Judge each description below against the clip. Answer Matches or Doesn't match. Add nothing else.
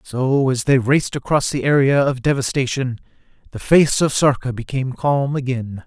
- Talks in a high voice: Doesn't match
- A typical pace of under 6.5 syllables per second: Matches